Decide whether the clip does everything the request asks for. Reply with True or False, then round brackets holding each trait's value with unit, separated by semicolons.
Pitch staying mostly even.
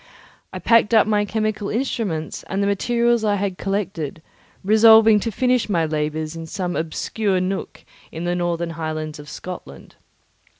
False (4.8 semitones)